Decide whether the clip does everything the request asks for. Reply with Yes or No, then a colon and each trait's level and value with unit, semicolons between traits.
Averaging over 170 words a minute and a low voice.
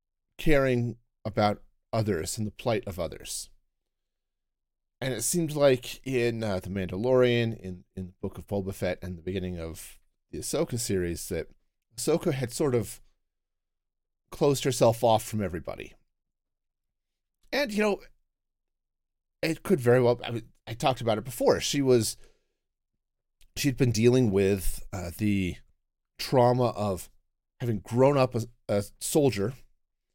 No: average, 140 wpm; low, 105 Hz